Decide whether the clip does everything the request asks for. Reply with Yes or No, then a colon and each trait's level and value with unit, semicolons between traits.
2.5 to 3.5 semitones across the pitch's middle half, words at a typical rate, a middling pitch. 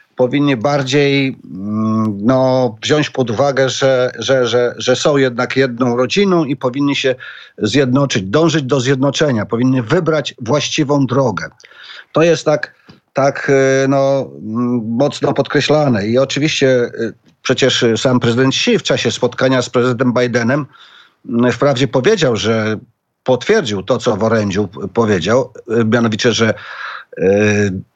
No: average, 2.8 semitones; average, 120 wpm; low, 130 Hz